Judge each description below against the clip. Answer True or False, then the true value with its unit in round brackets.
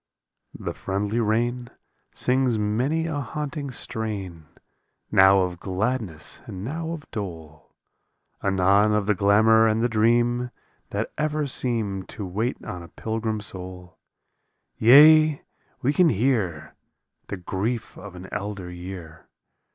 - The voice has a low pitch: True (110 Hz)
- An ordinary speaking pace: False (130 wpm)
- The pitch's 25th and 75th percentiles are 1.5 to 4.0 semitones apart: False (4.6 semitones)